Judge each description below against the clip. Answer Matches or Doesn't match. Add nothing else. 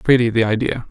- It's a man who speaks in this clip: Matches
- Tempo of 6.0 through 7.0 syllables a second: Matches